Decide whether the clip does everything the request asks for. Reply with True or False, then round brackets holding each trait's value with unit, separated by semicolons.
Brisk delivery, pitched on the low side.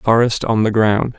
True (250 wpm; 115 Hz)